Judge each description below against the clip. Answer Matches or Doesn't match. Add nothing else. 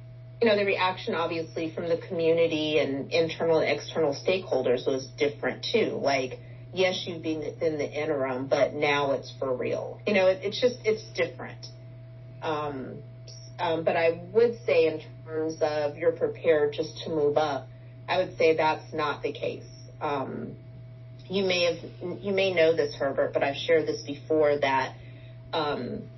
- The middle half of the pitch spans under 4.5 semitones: Doesn't match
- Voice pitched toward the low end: Doesn't match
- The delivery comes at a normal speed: Matches